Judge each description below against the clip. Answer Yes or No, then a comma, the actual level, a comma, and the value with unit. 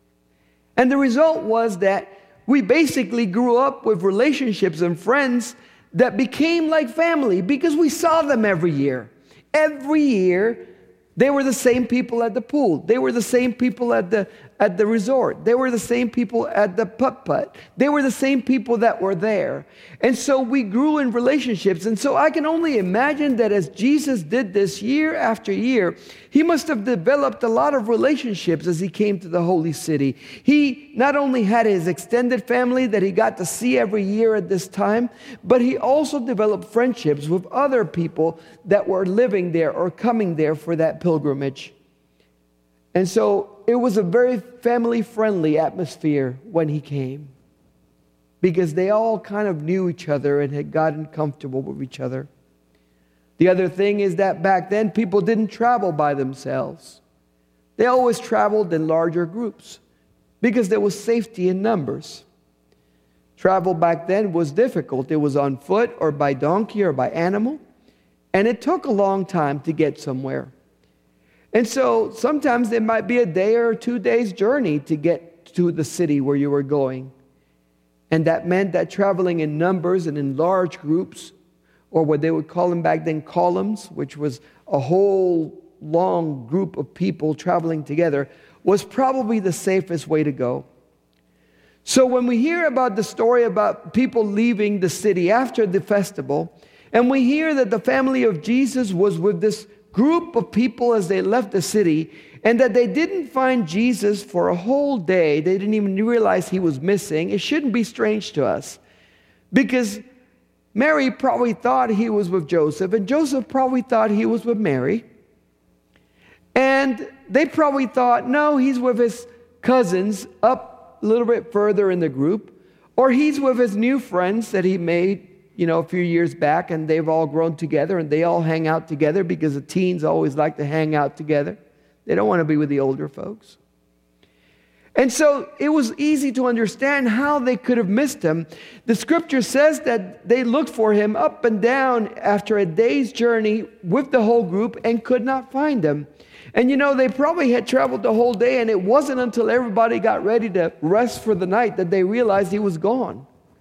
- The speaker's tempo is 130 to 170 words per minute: No, average, 180 wpm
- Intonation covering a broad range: Yes, wide, 7.0 semitones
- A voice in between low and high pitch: No, high, 205 Hz